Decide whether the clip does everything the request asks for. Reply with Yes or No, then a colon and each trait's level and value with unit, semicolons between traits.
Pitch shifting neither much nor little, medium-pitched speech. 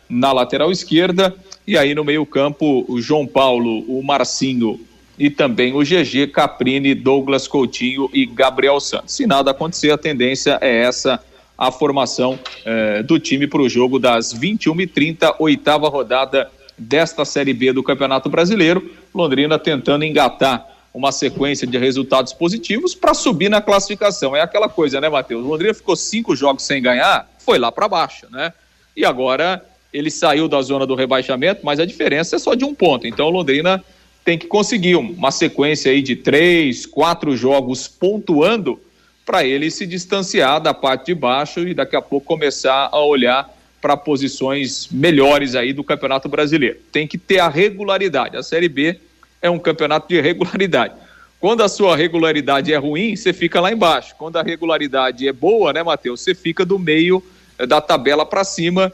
Yes: average, 4.7 semitones; medium, 150 Hz